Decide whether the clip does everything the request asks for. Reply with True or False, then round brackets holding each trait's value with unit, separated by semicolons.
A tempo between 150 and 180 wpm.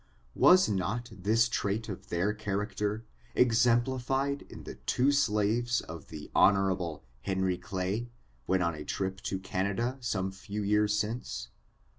False (135 wpm)